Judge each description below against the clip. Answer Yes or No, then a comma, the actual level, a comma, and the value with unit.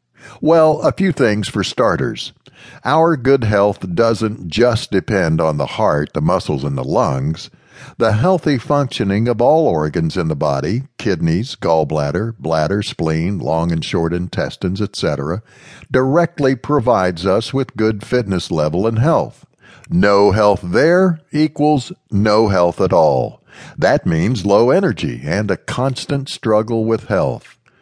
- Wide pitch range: Yes, wide, 7.4 semitones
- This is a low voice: Yes, low, 110 Hz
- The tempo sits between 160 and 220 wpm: No, average, 140 wpm